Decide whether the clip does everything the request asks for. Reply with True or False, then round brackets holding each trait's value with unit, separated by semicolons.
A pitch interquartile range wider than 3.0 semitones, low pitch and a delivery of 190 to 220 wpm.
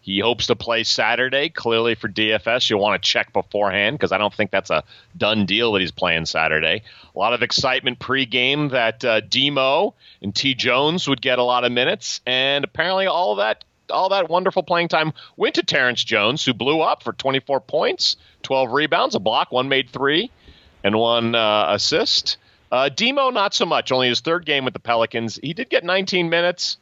True (4.7 semitones; 125 Hz; 200 wpm)